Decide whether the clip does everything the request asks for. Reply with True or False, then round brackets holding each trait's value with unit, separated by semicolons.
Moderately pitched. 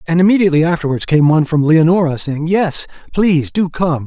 True (165 Hz)